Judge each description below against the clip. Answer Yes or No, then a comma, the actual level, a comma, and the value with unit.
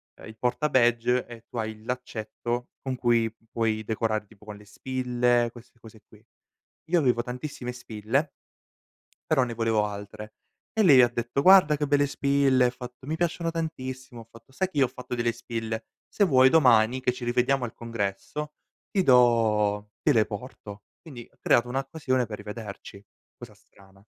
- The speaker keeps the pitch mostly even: No, average, 3.0 semitones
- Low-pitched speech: Yes, low, 120 Hz